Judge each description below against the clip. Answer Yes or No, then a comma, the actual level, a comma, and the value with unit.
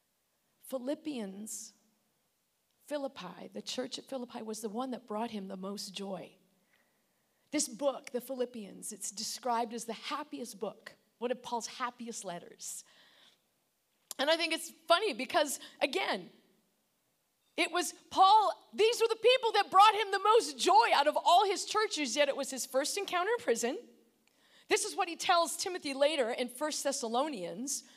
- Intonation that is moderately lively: No, wide, 6.8 semitones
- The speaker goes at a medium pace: Yes, average, 155 wpm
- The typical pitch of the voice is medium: No, very high, 275 Hz